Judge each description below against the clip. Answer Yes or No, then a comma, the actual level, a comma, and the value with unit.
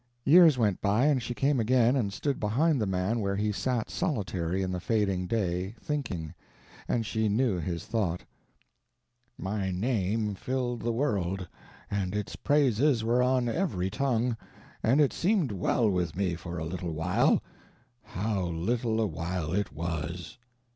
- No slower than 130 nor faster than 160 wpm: Yes, average, 155 wpm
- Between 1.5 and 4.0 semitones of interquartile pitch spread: No, average, 5.3 semitones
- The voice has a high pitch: No, low, 105 Hz